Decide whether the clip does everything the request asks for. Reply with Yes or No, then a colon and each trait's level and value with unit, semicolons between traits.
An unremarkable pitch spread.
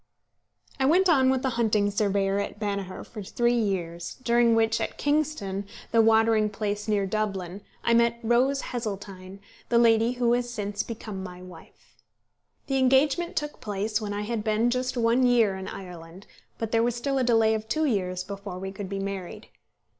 Yes: average, 3.3 semitones